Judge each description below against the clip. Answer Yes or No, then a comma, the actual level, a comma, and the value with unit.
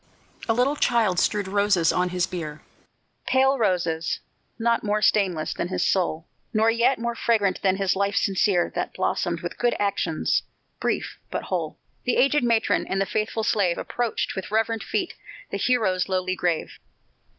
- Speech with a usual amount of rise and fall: Yes, average, 4.0 semitones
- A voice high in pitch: Yes, high, 200 Hz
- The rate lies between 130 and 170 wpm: Yes, average, 160 wpm